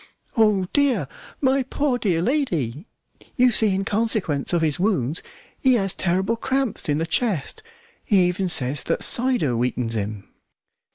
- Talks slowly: No, average, 150 wpm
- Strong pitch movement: Yes, wide, 8.4 semitones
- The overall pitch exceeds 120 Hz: Yes, high, 190 Hz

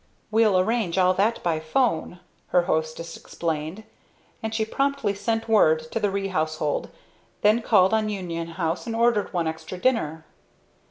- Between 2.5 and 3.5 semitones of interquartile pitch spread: No, average, 5.2 semitones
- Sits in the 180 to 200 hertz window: Yes, high, 190 Hz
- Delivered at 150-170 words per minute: Yes, average, 155 wpm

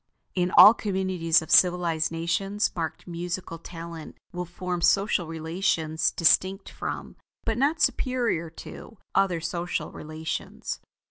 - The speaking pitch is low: No, medium, 175 Hz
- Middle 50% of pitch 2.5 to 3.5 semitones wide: Yes, average, 2.8 semitones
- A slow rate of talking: Yes, slow, 120 wpm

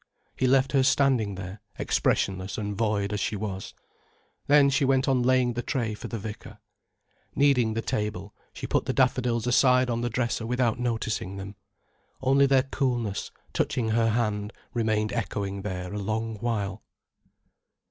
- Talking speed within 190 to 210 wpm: No, average, 160 wpm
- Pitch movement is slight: No, average, 3.6 semitones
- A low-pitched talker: Yes, low, 115 Hz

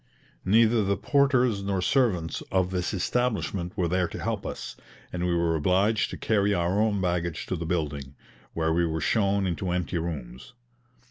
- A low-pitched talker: Yes, very low, 90 Hz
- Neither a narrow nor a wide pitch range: Yes, average, 3.2 semitones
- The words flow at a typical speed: Yes, average, 175 wpm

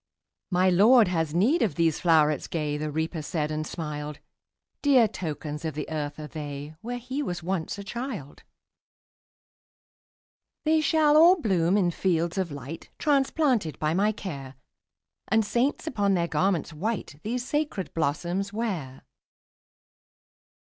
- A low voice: No, medium, 180 Hz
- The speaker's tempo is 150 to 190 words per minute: No, average, 140 wpm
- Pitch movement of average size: No, wide, 6.7 semitones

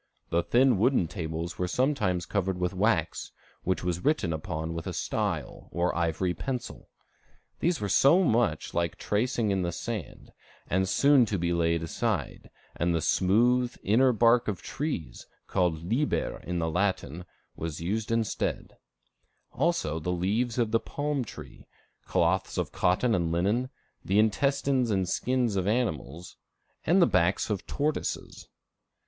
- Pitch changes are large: Yes, wide, 6.1 semitones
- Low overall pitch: Yes, low, 100 Hz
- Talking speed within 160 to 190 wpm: No, average, 150 wpm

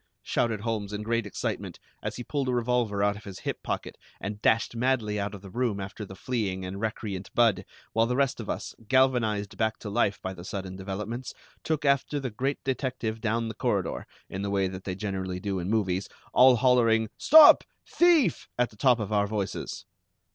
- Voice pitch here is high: No, low, 110 Hz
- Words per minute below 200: No, fast, 205 wpm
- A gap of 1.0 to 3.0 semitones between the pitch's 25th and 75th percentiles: No, average, 3.7 semitones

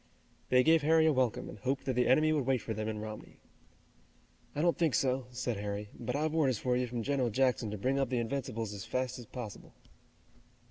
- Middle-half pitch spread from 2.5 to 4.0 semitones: Yes, average, 3.5 semitones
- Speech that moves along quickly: Yes, fast, 220 wpm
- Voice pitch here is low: Yes, low, 125 Hz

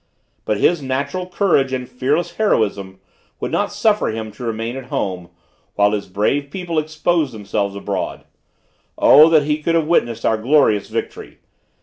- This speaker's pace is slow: No, average, 155 wpm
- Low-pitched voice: Yes, low, 130 Hz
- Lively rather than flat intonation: Yes, wide, 6.7 semitones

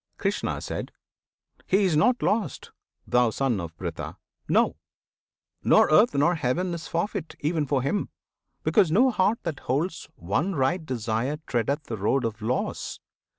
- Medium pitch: Yes, medium, 145 Hz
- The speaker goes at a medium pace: Yes, average, 145 wpm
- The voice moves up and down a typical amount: No, wide, 6.9 semitones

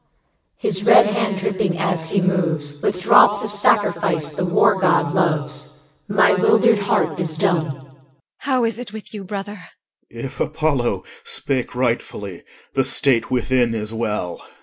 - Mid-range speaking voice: Yes, medium, 170 Hz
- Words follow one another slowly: No, average, 155 wpm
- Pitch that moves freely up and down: Yes, wide, 6.5 semitones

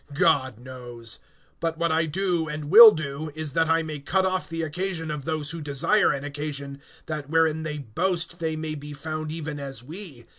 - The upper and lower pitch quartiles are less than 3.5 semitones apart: Yes, narrow, 2.4 semitones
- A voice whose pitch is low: No, medium, 155 Hz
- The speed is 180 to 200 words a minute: Yes, average, 195 wpm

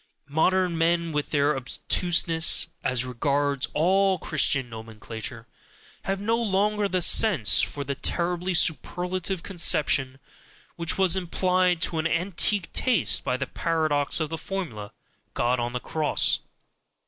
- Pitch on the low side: No, medium, 165 Hz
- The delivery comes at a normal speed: No, slow, 130 wpm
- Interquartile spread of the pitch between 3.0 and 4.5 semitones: No, average, 4.9 semitones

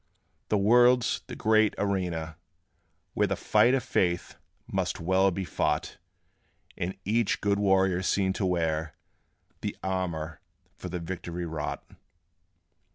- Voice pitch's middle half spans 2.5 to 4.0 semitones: Yes, average, 2.8 semitones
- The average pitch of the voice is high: No, very low, 95 Hz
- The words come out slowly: Yes, slow, 125 wpm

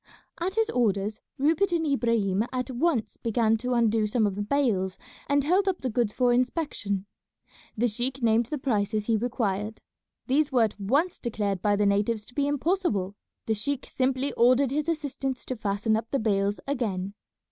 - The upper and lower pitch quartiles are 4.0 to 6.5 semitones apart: Yes, average, 4.9 semitones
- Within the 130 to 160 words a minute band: No, average, 180 wpm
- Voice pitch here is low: No, high, 235 Hz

